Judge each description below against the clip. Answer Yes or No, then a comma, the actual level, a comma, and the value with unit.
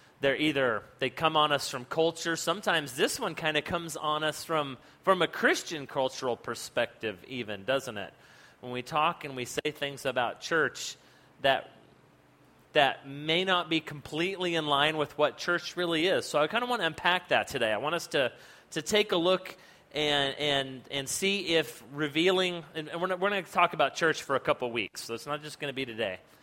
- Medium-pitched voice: Yes, medium, 155 Hz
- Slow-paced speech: No, fast, 205 wpm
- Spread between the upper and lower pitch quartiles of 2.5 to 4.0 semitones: Yes, average, 3.7 semitones